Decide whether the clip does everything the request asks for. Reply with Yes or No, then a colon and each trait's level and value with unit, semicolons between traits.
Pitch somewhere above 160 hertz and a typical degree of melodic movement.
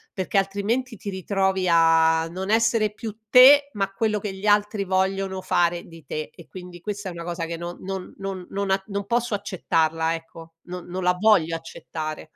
Yes: high, 190 Hz; average, 3.3 semitones